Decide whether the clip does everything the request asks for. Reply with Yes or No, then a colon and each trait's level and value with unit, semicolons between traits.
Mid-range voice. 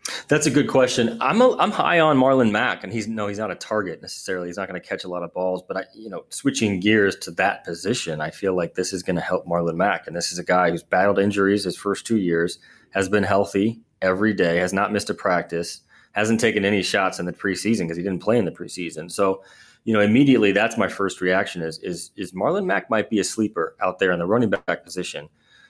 No: low, 100 Hz